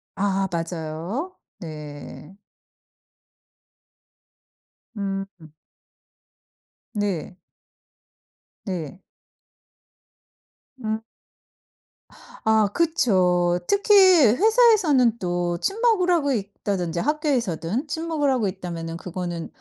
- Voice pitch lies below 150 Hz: No, high, 200 Hz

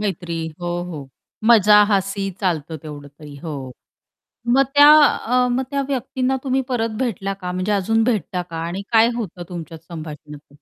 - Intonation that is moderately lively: No, wide, 6.0 semitones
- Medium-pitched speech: No, high, 195 Hz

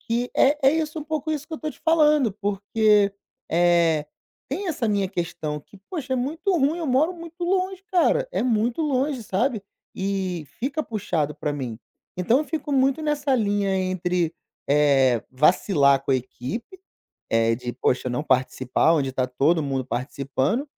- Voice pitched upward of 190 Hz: Yes, high, 205 Hz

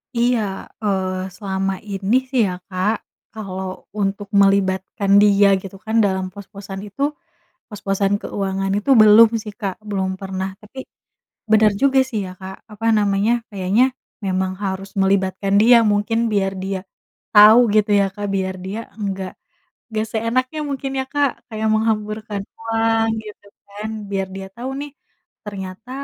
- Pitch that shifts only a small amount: Yes, narrow, 2.2 semitones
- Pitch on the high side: Yes, high, 200 Hz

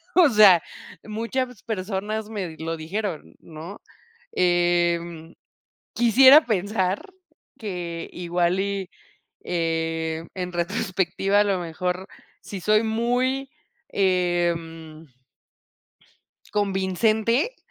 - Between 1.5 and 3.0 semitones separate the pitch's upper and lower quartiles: No, average, 3.8 semitones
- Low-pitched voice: No, high, 190 Hz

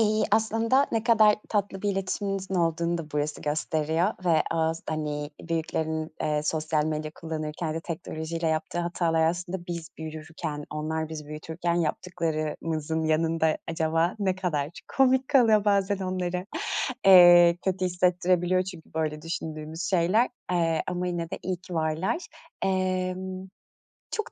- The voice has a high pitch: No, medium, 170 Hz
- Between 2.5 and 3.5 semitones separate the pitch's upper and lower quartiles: Yes, average, 2.8 semitones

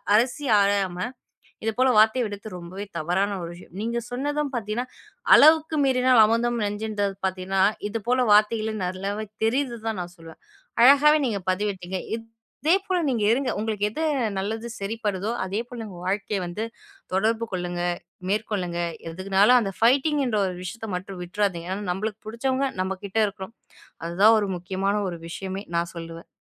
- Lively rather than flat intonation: No, average, 3.8 semitones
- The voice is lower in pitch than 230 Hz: Yes, high, 210 Hz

